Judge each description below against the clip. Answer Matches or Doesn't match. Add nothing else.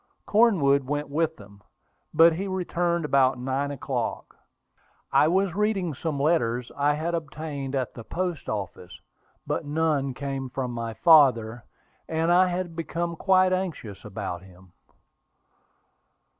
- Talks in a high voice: Doesn't match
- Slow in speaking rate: Matches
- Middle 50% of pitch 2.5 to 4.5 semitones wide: Doesn't match